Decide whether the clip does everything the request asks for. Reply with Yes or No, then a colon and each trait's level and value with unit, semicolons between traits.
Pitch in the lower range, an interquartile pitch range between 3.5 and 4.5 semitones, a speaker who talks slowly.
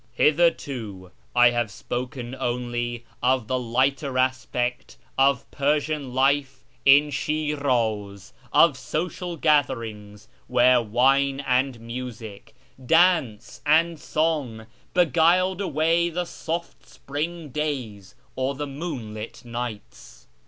Yes: low, 130 Hz; average, 4.1 semitones; slow, 105 wpm